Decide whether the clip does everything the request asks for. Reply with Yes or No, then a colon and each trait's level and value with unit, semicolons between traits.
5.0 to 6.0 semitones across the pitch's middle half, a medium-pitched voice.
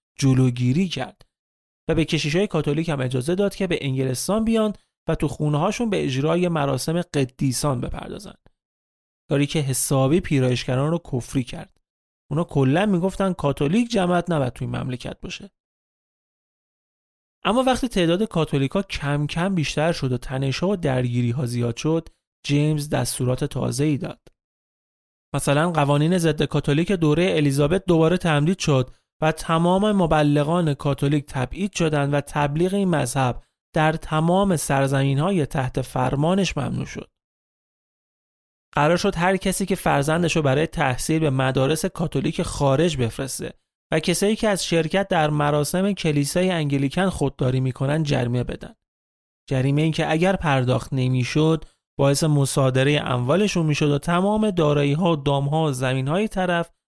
No: average, 4.3 semitones; medium, 150 Hz